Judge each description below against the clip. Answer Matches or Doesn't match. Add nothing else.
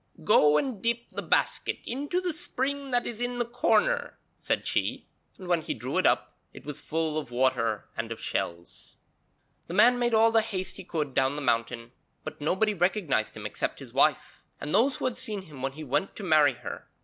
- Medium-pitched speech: Matches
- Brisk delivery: Matches